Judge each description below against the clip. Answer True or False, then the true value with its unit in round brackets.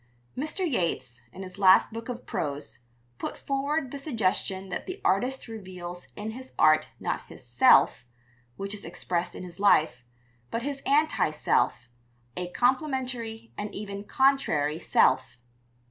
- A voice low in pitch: False (210 Hz)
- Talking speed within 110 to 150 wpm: True (145 wpm)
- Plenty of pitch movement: True (6.7 semitones)